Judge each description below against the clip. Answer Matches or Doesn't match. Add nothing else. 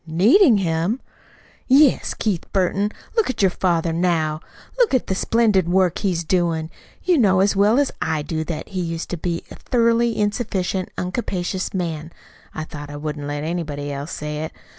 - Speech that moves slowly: Doesn't match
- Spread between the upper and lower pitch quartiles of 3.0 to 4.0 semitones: Doesn't match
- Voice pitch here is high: Doesn't match